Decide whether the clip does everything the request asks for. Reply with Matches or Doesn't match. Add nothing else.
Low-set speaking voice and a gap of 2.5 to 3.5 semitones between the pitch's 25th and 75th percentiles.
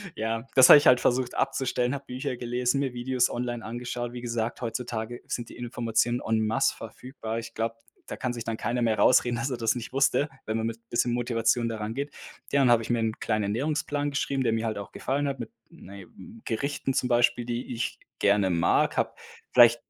Doesn't match